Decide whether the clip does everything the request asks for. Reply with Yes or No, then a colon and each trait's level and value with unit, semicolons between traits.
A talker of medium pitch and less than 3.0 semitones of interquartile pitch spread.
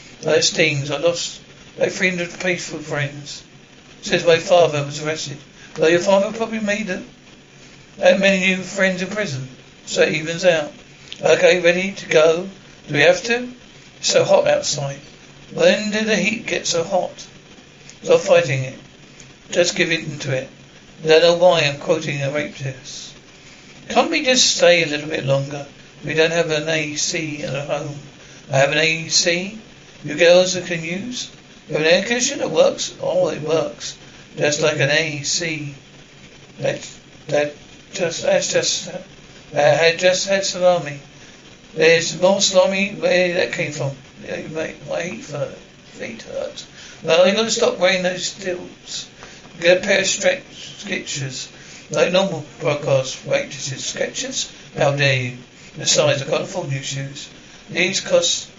No: medium, 170 Hz; average, 4.4 semitones